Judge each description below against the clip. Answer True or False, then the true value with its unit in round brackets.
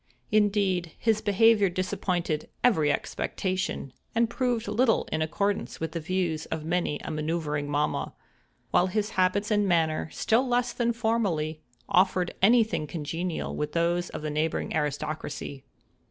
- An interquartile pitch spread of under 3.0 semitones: False (5.1 semitones)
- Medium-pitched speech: True (180 Hz)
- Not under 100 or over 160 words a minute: True (140 wpm)